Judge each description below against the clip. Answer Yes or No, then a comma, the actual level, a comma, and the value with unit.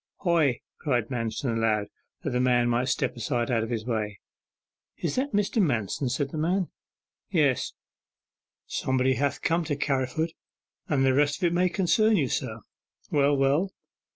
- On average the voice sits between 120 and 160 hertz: Yes, low, 135 Hz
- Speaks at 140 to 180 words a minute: Yes, average, 160 wpm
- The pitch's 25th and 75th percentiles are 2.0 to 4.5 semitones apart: No, average, 5.2 semitones